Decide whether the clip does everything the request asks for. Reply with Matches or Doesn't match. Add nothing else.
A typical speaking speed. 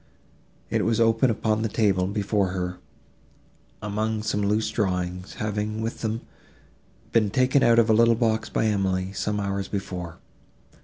Matches